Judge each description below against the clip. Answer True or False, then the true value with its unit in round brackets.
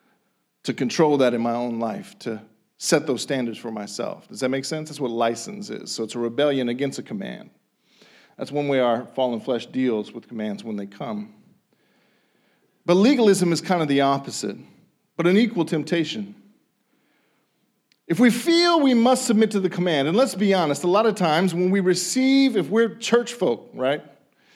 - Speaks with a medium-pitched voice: True (160 Hz)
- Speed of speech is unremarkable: True (185 wpm)